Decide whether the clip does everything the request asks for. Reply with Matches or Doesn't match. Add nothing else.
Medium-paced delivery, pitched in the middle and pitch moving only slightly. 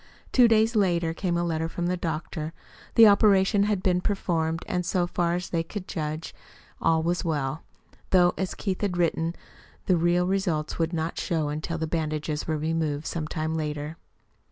Matches